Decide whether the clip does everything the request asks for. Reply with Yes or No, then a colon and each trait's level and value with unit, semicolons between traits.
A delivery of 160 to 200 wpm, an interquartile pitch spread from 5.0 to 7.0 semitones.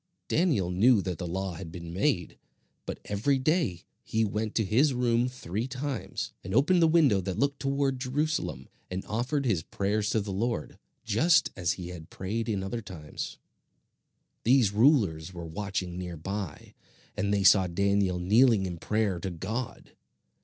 Yes: average, 165 wpm; wide, 5.6 semitones